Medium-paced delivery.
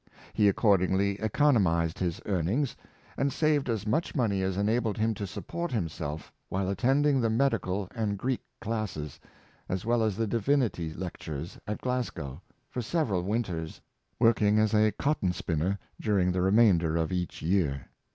Yes: average, 150 wpm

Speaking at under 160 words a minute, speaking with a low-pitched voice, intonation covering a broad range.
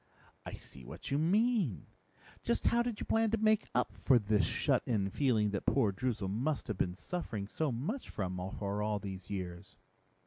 No: average, 185 wpm; low, 110 Hz; wide, 8.4 semitones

